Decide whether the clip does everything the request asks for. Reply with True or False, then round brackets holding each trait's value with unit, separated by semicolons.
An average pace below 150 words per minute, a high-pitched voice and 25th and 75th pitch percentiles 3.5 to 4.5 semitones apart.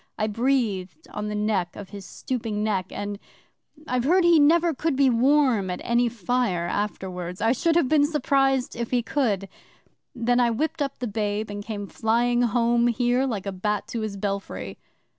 False (180 wpm; 230 Hz; 4.2 semitones)